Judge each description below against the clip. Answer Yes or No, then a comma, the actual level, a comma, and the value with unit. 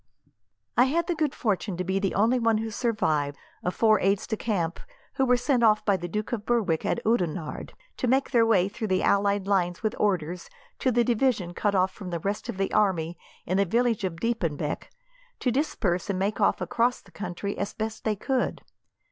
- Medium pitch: No, high, 205 Hz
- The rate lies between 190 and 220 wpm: Yes, fast, 205 wpm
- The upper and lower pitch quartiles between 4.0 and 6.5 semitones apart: Yes, average, 4.3 semitones